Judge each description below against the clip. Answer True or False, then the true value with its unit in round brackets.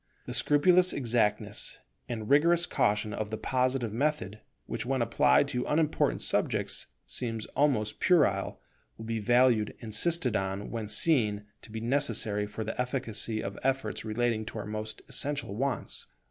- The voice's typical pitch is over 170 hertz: False (115 Hz)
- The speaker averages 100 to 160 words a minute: True (150 wpm)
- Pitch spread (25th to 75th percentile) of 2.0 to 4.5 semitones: True (4.2 semitones)